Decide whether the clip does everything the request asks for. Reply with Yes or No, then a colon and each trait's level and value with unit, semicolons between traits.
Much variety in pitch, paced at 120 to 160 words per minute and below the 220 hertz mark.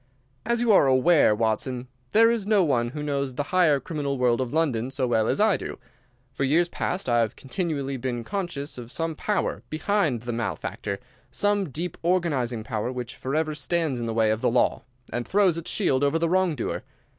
No: wide, 6.1 semitones; average, 200 wpm; medium, 140 Hz